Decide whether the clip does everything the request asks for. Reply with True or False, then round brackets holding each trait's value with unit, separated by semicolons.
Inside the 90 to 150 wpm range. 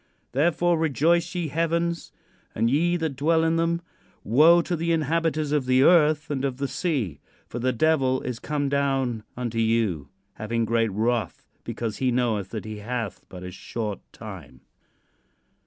False (160 wpm)